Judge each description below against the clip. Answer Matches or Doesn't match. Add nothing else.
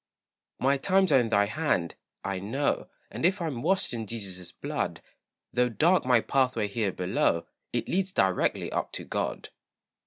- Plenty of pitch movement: Matches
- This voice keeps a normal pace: Matches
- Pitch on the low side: Matches